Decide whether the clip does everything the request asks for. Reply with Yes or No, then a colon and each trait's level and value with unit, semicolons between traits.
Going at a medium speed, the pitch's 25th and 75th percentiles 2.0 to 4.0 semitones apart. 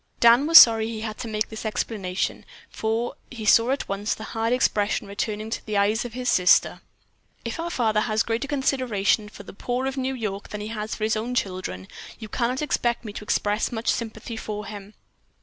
No: fast, 210 wpm; narrow, 2.4 semitones